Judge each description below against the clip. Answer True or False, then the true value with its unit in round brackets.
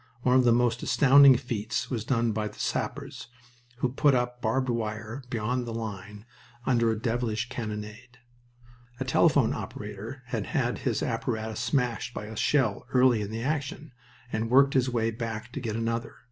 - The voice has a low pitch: True (115 Hz)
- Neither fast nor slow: True (170 wpm)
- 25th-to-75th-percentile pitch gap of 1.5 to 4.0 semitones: True (2.4 semitones)